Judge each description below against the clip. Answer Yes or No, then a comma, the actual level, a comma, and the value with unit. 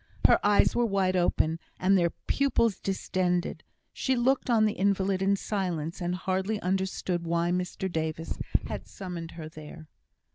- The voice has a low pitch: No, medium, 185 Hz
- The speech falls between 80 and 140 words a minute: No, average, 150 wpm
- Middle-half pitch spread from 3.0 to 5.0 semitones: No, narrow, 2.5 semitones